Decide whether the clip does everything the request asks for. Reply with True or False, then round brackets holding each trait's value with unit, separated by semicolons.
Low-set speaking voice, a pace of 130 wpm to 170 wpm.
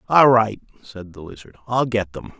False (110 Hz; 200 wpm)